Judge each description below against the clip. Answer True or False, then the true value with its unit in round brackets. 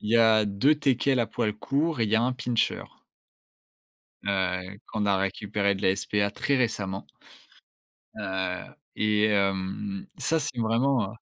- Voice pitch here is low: True (105 Hz)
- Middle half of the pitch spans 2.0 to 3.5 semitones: False (4.1 semitones)